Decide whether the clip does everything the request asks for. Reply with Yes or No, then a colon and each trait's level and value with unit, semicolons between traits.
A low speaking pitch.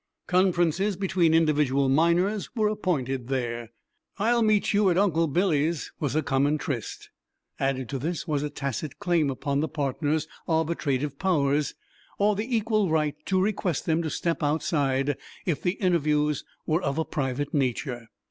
No: medium, 155 Hz